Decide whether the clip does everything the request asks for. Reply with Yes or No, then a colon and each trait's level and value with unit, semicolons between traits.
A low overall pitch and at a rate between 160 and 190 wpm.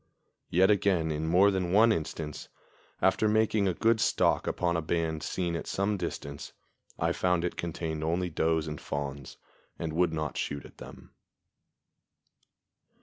No: very low, 85 Hz; average, 150 wpm